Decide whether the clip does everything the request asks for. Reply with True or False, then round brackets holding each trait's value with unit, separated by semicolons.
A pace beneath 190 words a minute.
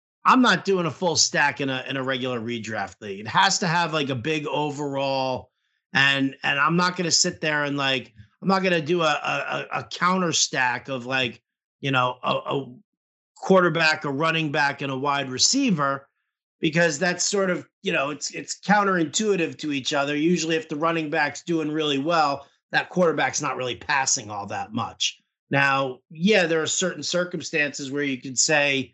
False (195 wpm)